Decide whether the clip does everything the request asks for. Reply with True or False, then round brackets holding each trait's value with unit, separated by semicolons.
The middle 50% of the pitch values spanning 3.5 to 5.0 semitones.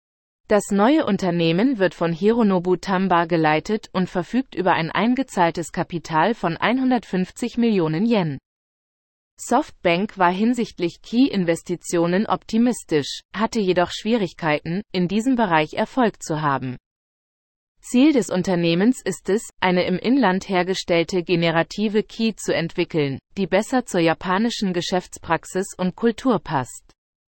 True (4.5 semitones)